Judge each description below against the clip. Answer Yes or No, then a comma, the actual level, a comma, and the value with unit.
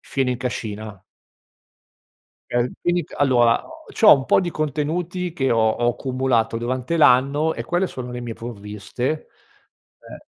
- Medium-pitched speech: No, low, 130 Hz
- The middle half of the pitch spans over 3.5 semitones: Yes, average, 4.7 semitones